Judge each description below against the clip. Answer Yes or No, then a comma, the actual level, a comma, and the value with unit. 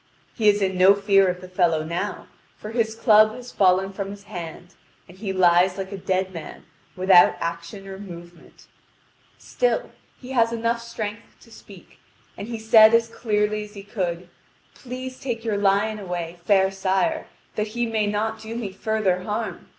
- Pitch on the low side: No, high, 200 Hz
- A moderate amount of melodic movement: Yes, average, 3.0 semitones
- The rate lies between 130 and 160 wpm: No, average, 175 wpm